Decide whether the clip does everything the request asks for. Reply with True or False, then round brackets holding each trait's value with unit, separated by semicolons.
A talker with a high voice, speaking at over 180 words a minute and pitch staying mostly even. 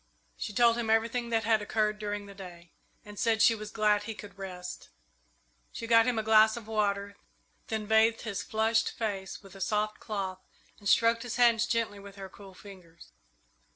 True (215 Hz; 190 wpm; 2.1 semitones)